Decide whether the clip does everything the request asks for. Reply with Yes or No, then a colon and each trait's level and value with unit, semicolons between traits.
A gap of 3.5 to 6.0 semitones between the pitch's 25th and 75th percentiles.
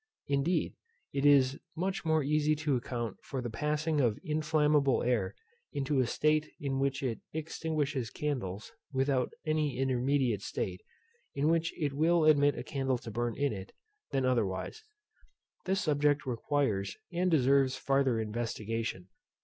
Yes: average, 3.8 semitones